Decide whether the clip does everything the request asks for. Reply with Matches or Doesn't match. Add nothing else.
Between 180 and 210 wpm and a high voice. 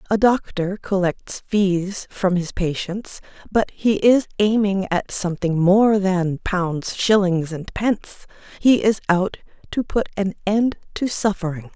Doesn't match